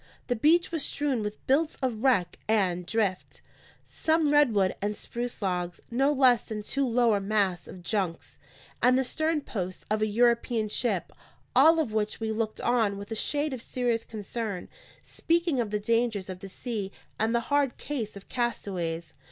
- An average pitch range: Yes, average, 4.3 semitones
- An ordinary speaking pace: Yes, average, 175 wpm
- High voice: Yes, high, 225 Hz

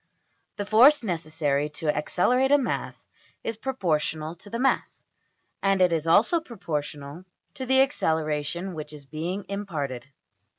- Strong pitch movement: Yes, wide, 6.7 semitones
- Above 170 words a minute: No, slow, 135 wpm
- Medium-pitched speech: Yes, medium, 175 Hz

